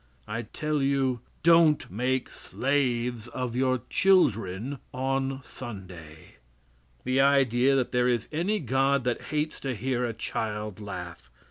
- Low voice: Yes, low, 130 Hz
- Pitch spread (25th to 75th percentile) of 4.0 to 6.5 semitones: No, average, 3.0 semitones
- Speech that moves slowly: Yes, slow, 130 wpm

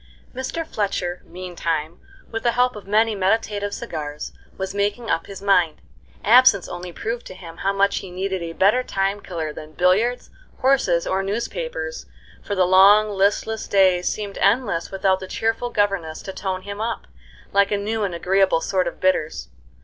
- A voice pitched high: Yes, high, 195 Hz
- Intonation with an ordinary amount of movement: Yes, average, 3.1 semitones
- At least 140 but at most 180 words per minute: Yes, average, 170 wpm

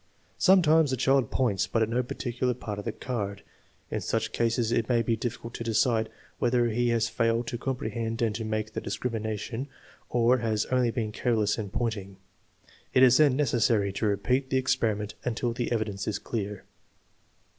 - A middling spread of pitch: No, narrow, 2.3 semitones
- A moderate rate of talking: Yes, average, 175 wpm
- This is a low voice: Yes, low, 115 Hz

